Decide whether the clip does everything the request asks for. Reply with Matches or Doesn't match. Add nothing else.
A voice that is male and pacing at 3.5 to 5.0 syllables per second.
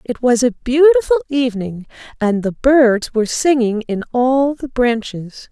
Doesn't match